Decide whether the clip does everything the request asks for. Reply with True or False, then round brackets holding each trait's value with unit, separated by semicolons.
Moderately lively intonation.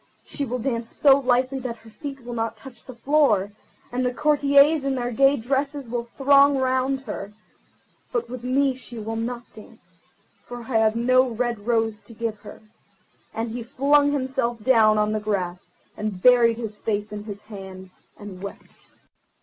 True (3.6 semitones)